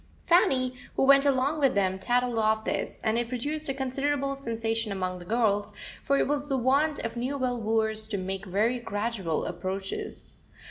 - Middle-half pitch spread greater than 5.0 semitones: No, average, 4.5 semitones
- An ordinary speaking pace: Yes, average, 175 wpm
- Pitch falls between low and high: No, high, 235 Hz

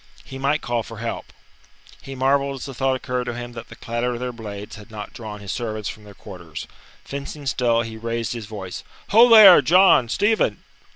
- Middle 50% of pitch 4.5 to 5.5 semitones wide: No, average, 3.4 semitones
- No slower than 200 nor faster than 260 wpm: Yes, fast, 205 wpm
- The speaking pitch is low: Yes, low, 120 Hz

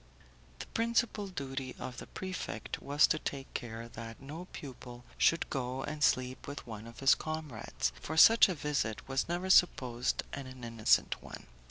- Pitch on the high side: No, low, 135 Hz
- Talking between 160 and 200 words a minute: Yes, average, 165 wpm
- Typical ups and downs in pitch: Yes, average, 4.6 semitones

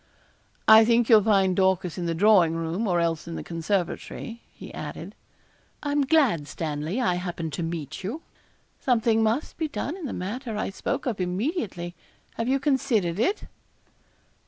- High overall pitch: Yes, high, 200 Hz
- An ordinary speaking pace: Yes, average, 165 wpm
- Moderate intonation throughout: No, wide, 5.9 semitones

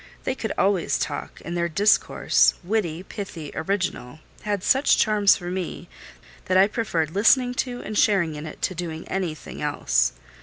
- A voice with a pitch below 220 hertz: Yes, medium, 185 Hz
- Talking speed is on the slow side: No, average, 160 wpm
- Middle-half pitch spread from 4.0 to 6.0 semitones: Yes, average, 4.3 semitones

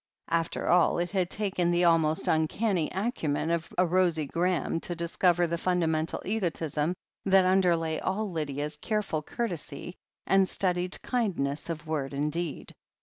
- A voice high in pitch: No, medium, 170 Hz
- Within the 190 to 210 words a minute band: No, average, 145 wpm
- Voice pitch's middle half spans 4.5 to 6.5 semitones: No, average, 2.7 semitones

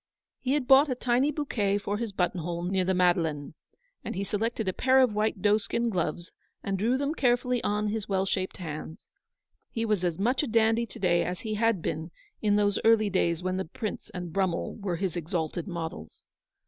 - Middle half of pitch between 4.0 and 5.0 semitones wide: Yes, average, 4.3 semitones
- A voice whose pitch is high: Yes, high, 200 Hz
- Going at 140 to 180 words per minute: No, average, 200 wpm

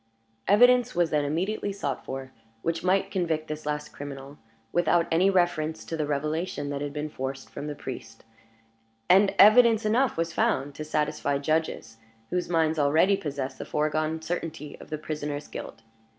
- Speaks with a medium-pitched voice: Yes, medium, 155 Hz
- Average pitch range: Yes, average, 3.8 semitones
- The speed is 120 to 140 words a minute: No, average, 165 wpm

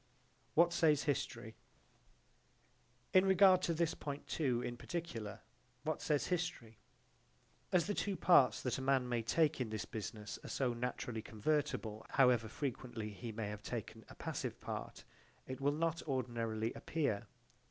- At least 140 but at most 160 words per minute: Yes, average, 150 wpm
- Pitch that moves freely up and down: Yes, wide, 5.8 semitones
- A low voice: Yes, low, 125 Hz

